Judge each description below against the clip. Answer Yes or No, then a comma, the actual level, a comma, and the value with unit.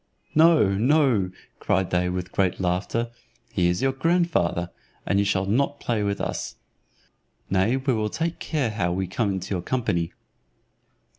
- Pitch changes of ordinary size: No, wide, 6.3 semitones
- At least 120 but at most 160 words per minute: Yes, average, 155 wpm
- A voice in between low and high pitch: No, low, 100 Hz